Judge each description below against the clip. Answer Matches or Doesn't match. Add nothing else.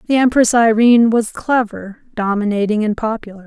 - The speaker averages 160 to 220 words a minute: Doesn't match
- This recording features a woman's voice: Matches